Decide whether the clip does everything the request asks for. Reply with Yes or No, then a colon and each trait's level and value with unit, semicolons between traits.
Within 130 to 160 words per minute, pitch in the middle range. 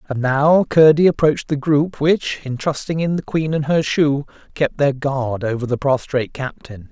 No: average, 190 wpm; medium, 145 Hz